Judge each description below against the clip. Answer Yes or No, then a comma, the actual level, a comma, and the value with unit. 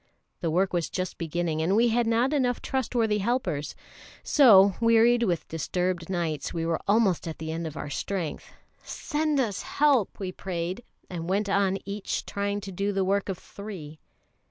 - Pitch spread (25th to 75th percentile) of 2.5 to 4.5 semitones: No, average, 5.0 semitones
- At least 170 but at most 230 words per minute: Yes, average, 175 wpm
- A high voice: Yes, high, 195 Hz